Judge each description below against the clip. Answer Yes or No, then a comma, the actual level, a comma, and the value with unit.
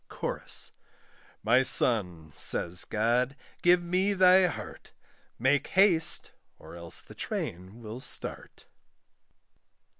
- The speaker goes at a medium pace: No, slow, 100 wpm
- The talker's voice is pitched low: Yes, low, 125 Hz